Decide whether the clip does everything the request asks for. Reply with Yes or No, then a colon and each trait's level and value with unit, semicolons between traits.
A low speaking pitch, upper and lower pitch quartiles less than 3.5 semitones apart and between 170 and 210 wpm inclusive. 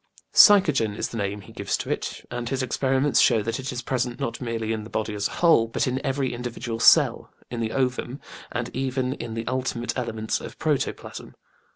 Yes: low, 120 Hz; average, 2.7 semitones; fast, 205 wpm